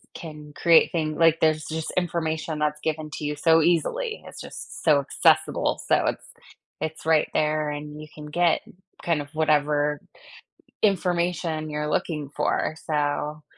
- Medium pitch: Yes, medium, 155 Hz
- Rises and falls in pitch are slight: Yes, narrow, 1.6 semitones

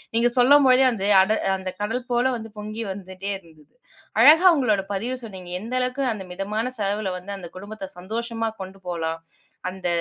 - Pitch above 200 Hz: Yes, high, 210 Hz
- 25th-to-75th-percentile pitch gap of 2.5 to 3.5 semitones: No, average, 4.0 semitones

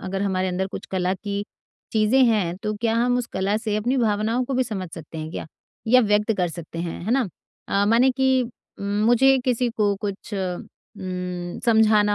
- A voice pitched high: Yes, high, 210 Hz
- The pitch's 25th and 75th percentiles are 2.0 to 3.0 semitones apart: No, average, 4.0 semitones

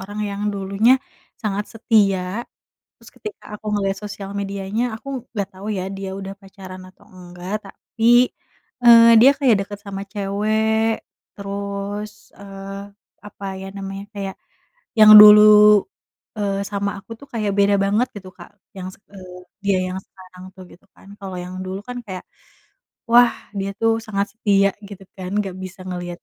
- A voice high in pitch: Yes, high, 200 Hz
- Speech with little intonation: Yes, narrow, 1.6 semitones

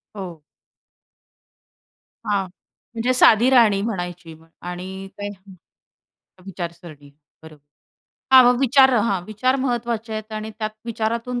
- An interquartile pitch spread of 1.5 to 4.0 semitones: No, average, 4.7 semitones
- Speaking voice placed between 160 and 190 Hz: No, high, 215 Hz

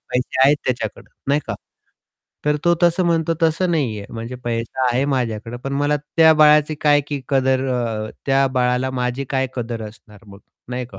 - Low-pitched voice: Yes, low, 130 Hz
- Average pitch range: Yes, average, 3.7 semitones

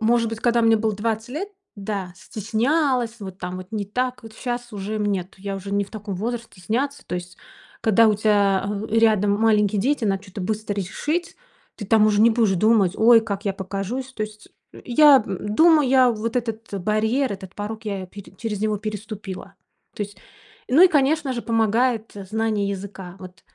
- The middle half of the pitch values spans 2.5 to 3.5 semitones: Yes, average, 2.8 semitones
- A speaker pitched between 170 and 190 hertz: No, high, 215 Hz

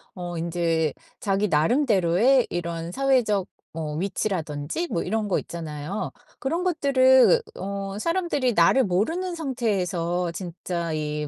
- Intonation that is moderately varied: No, wide, 7.5 semitones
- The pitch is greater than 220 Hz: No, high, 195 Hz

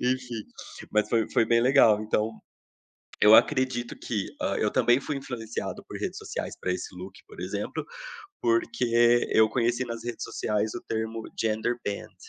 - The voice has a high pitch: No, low, 115 Hz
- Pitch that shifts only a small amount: Yes, narrow, 2.1 semitones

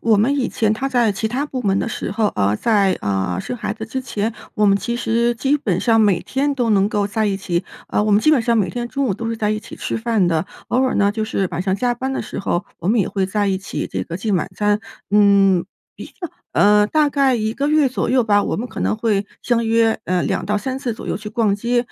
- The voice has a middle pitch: No, high, 215 Hz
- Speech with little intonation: No, average, 3.3 semitones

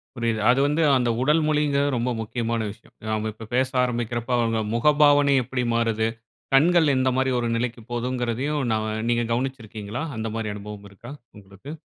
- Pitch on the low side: Yes, low, 120 Hz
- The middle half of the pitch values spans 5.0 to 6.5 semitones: No, average, 3.4 semitones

